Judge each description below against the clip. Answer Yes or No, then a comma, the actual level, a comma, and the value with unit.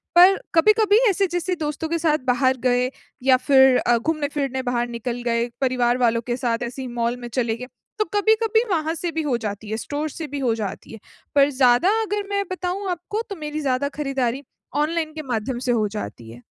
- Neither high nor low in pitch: No, very high, 270 Hz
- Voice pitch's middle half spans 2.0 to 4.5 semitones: No, wide, 5.4 semitones